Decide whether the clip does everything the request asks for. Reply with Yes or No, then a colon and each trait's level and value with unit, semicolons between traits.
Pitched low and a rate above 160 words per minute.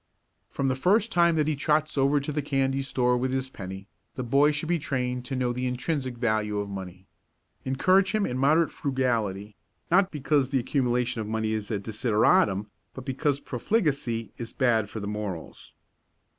Yes: low, 130 Hz; average, 180 wpm